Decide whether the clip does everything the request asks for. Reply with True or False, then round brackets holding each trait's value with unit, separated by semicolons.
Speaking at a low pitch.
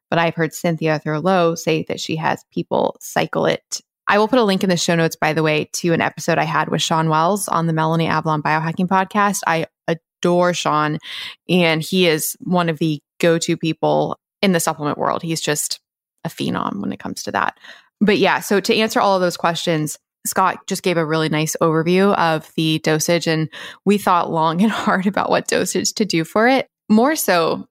False (165 Hz)